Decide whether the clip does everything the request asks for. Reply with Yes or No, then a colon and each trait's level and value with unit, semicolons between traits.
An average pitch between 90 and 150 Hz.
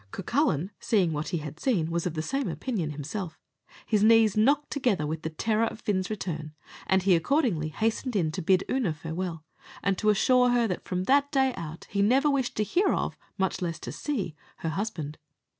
No: high, 195 Hz